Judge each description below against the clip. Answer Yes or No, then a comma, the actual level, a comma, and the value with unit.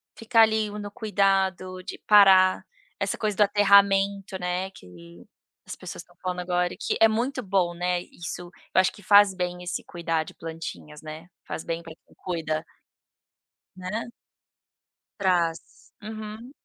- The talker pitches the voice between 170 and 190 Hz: Yes, medium, 185 Hz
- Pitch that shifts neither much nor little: Yes, average, 3.0 semitones